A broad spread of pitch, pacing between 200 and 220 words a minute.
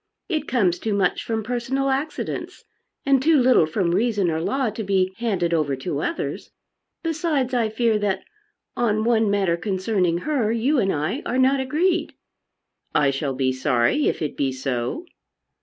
No: wide, 7.2 semitones; average, 165 wpm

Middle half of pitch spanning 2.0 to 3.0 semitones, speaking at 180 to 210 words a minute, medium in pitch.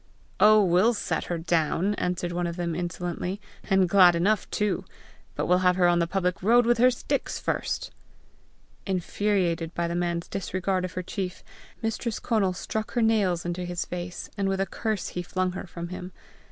Yes: narrow, 2.5 semitones; average, 190 wpm; medium, 180 Hz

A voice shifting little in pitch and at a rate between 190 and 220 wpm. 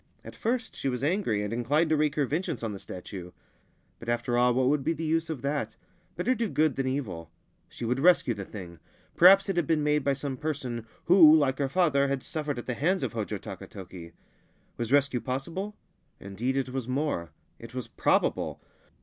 No: average, 5.0 semitones; average, 200 wpm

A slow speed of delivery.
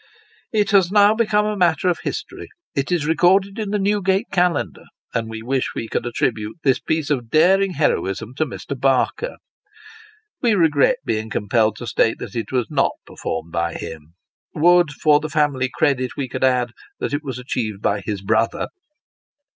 No: average, 175 wpm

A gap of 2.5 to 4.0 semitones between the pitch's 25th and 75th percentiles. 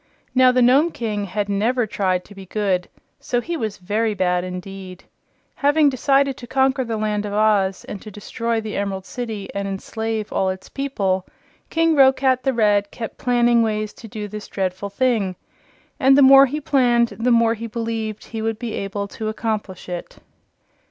Yes: average, 3.7 semitones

